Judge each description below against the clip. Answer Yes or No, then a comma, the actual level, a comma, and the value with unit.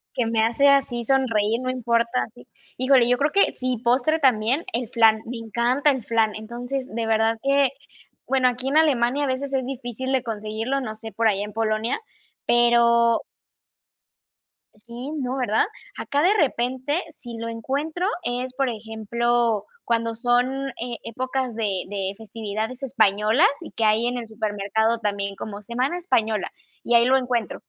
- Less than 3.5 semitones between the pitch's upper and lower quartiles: Yes, average, 2.7 semitones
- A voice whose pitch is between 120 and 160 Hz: No, high, 235 Hz